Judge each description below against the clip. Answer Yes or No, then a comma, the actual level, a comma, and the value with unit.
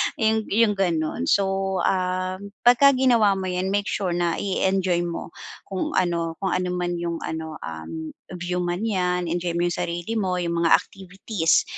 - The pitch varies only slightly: Yes, narrow, 2.1 semitones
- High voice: No, medium, 180 Hz